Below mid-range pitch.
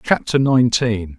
Yes: low, 110 Hz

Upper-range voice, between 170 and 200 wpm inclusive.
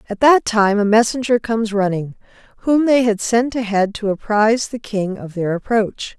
Yes: high, 220 Hz; average, 185 wpm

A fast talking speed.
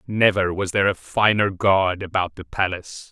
No: average, 175 wpm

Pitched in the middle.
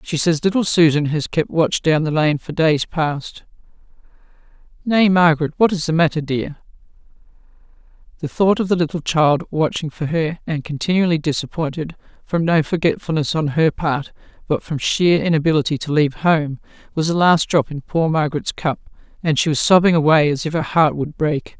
Yes: medium, 160 Hz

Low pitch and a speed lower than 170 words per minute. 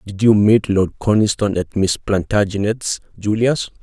Yes: low, 105 Hz; average, 140 wpm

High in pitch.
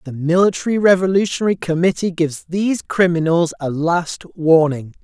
No: medium, 175 Hz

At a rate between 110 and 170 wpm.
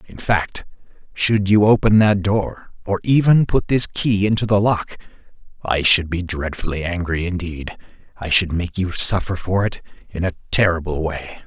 Yes: average, 165 wpm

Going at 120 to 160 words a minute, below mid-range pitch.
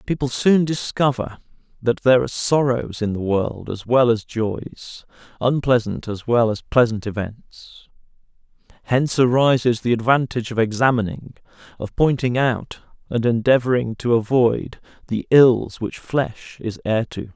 Yes: average, 140 wpm; low, 120 Hz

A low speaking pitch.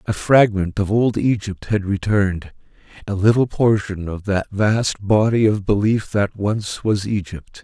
Yes: low, 100 Hz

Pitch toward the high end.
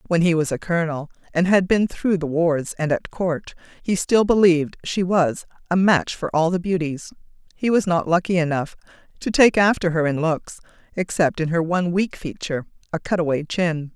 No: medium, 170 Hz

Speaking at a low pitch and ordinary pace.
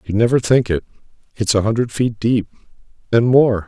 Yes: low, 110 Hz; average, 145 wpm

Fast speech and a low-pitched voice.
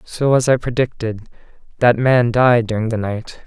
No: average, 175 wpm; low, 120 Hz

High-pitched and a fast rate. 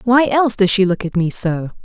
Yes: high, 205 Hz; fast, 260 wpm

